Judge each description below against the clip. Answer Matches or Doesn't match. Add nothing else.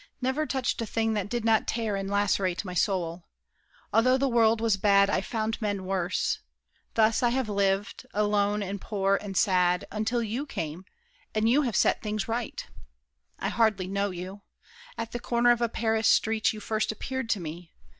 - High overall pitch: Matches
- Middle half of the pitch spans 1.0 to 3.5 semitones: Matches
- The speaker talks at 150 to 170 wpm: Doesn't match